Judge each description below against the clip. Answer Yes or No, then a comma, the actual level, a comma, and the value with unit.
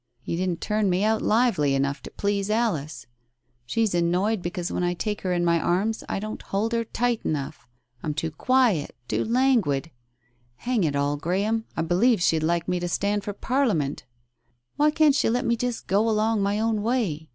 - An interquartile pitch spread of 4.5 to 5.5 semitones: Yes, average, 5.1 semitones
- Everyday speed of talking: Yes, average, 190 wpm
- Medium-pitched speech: No, high, 200 Hz